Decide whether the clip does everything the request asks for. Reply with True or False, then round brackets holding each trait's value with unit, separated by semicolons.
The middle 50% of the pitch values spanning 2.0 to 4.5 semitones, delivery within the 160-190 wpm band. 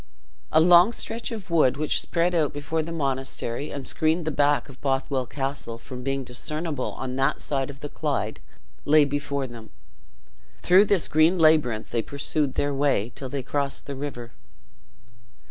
True (3.0 semitones; 165 wpm)